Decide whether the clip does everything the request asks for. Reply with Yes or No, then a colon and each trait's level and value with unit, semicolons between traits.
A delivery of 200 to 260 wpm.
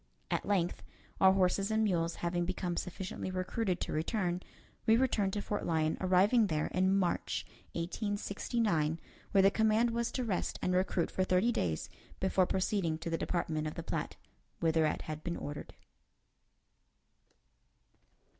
No: average, 150 wpm